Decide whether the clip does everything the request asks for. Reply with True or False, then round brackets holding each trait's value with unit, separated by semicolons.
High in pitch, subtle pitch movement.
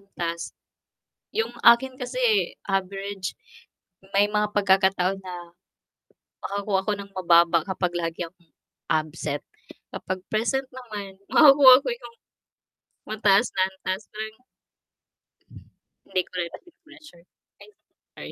False (195 Hz; 3.7 semitones)